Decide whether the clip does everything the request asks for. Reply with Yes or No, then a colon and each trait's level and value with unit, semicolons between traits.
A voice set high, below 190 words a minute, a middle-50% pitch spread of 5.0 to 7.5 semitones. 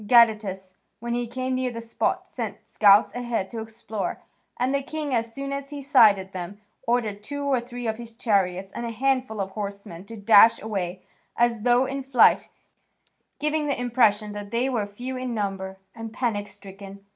No: high, 230 Hz; average, 180 wpm; average, 3.8 semitones